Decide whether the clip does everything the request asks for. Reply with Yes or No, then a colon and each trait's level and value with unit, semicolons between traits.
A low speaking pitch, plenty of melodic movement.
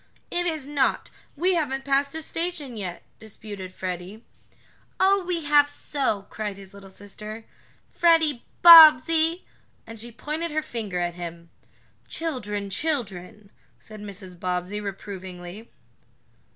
No: high, 220 Hz; wide, 7.9 semitones